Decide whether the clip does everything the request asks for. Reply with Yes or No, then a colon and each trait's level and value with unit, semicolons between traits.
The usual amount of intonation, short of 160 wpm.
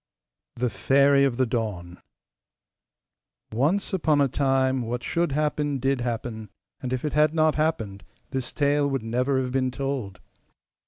Yes: average, 3.2 semitones; average, 150 wpm